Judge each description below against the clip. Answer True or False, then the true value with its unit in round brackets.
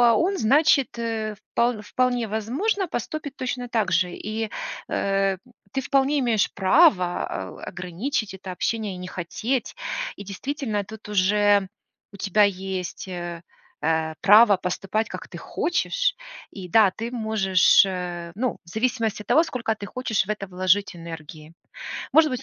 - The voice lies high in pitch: True (210 Hz)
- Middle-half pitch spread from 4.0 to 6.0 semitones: True (4.8 semitones)